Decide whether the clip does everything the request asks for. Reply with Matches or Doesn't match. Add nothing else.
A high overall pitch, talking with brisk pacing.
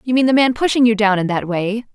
Matches